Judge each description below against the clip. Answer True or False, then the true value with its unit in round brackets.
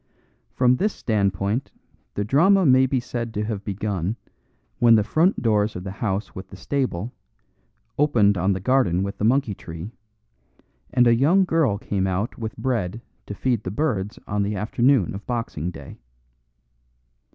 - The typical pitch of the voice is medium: False (110 Hz)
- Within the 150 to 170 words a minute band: True (165 wpm)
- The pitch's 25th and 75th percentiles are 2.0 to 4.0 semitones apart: False (4.5 semitones)